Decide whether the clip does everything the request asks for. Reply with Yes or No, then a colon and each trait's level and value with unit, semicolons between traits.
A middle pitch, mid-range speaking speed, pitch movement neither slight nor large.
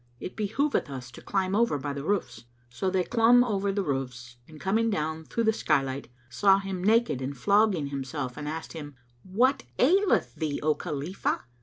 No: medium, 175 Hz; average, 190 wpm; wide, 6.9 semitones